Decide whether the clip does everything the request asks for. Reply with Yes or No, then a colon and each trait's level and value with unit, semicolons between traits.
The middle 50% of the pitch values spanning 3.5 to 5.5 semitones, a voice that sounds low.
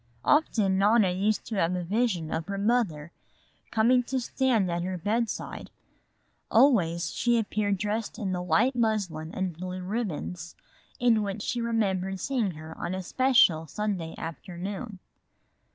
No: average, 4.3 semitones; high, 200 Hz